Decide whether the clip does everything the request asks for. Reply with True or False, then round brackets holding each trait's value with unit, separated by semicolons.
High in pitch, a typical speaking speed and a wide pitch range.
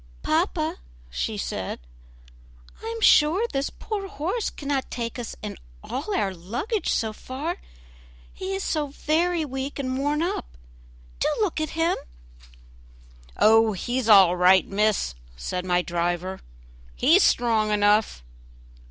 False (255 Hz; 130 wpm; 8.0 semitones)